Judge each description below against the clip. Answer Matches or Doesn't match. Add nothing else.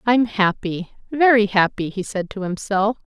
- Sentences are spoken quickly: Doesn't match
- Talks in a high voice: Matches